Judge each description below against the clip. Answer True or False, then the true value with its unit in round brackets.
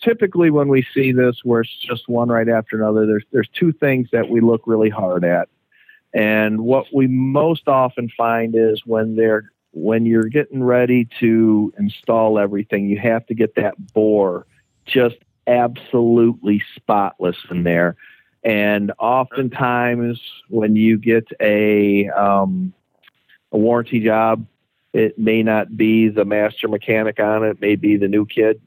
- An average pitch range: False (2.2 semitones)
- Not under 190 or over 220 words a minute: False (155 wpm)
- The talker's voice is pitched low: True (110 Hz)